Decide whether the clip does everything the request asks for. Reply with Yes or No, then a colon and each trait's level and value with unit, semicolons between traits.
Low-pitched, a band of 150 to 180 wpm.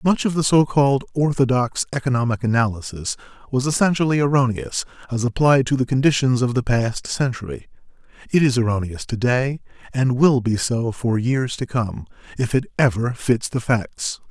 Yes: low, 125 Hz; average, 160 wpm